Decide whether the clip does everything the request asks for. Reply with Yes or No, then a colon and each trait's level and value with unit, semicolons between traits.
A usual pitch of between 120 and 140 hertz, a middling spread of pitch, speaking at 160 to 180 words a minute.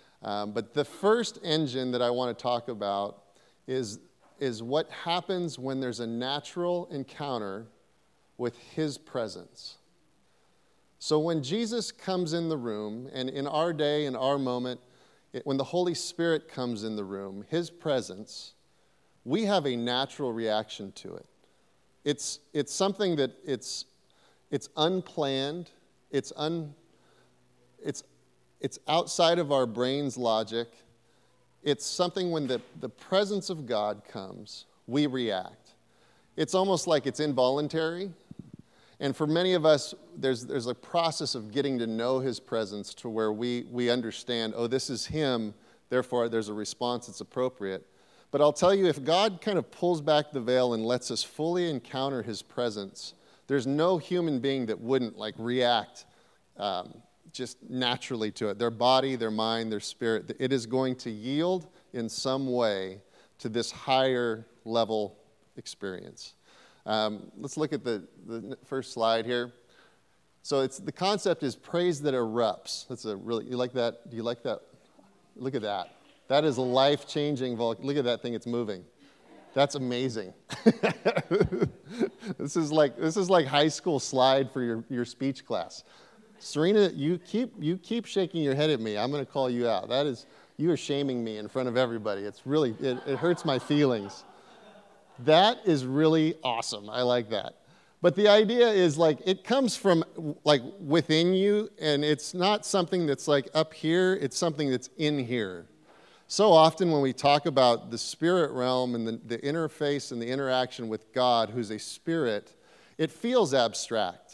Yes: low, 135 Hz; average, 5.0 semitones; average, 165 wpm